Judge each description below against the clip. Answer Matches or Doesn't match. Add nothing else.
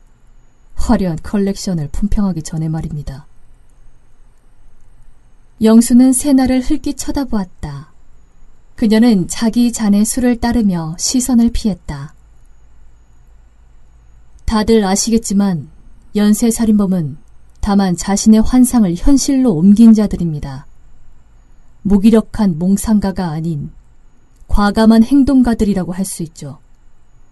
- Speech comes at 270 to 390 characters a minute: Doesn't match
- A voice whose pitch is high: Matches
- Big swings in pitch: Matches